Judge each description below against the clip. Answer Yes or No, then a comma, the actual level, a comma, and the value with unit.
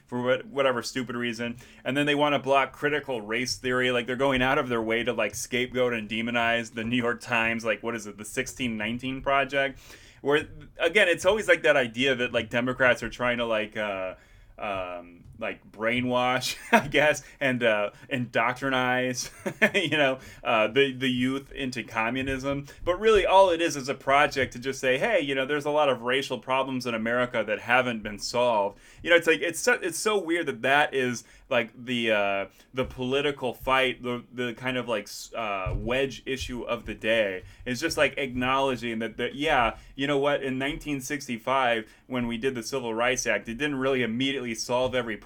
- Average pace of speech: Yes, average, 195 wpm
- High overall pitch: No, low, 125 Hz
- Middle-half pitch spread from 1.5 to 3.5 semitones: Yes, narrow, 2.6 semitones